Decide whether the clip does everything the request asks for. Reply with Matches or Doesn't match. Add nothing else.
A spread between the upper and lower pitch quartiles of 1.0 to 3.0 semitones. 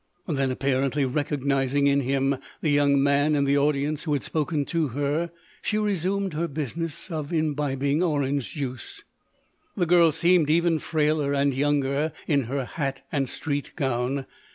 Matches